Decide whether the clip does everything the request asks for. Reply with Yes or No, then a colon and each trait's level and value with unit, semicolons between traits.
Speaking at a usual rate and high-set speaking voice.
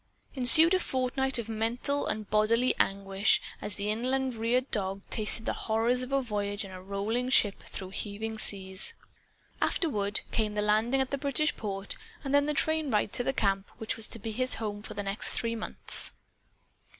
Yes: average, 185 wpm; high, 225 Hz